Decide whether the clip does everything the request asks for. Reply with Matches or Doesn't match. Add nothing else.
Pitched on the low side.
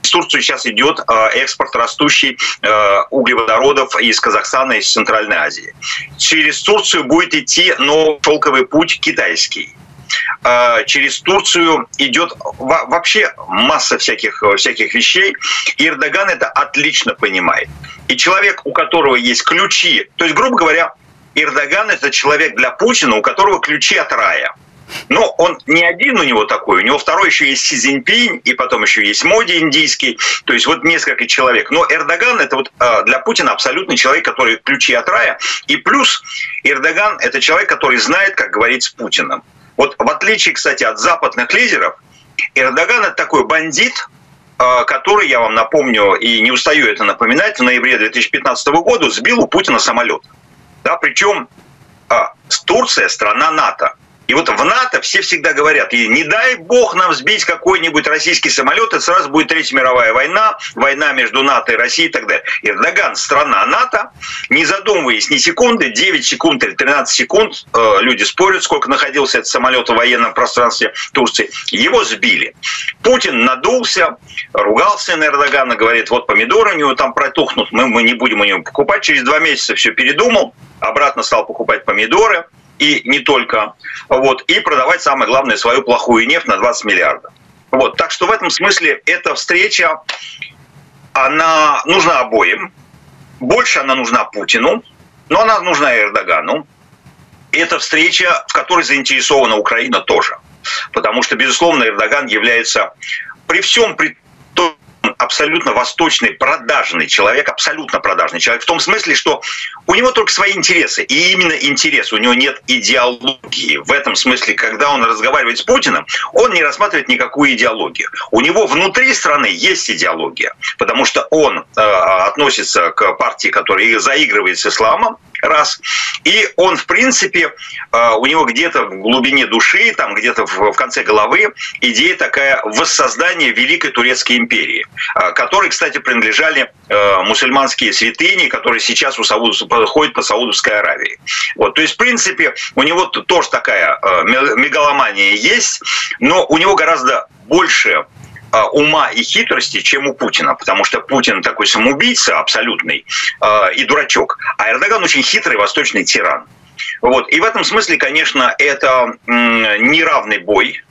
Doesn't match